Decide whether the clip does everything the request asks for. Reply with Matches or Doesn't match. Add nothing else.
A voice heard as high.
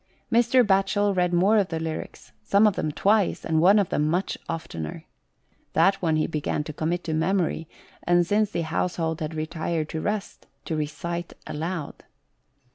Doesn't match